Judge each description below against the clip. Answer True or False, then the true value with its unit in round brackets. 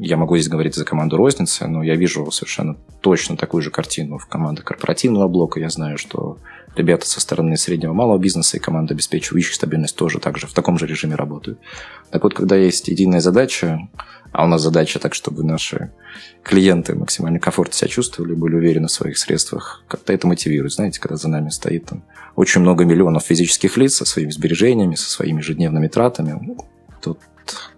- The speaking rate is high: True (185 wpm)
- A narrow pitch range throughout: True (2.1 semitones)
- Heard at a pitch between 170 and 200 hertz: False (80 Hz)